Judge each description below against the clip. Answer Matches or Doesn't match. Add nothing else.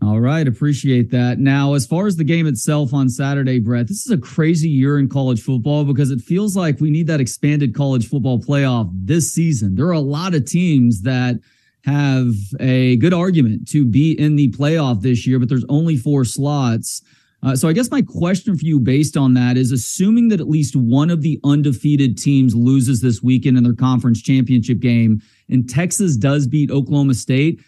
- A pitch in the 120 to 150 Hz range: Matches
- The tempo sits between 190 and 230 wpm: Matches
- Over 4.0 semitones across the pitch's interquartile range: Doesn't match